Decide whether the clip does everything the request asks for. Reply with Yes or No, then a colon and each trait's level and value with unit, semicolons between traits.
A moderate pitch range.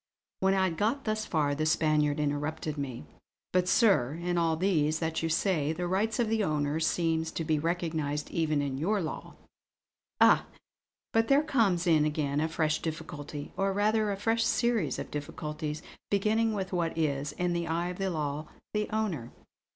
Yes: average, 4.4 semitones